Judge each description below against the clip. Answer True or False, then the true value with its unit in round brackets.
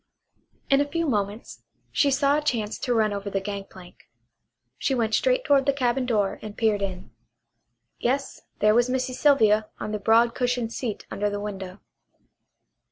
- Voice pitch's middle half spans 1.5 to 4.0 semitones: False (4.5 semitones)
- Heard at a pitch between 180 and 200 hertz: False (225 Hz)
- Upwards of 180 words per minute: False (165 wpm)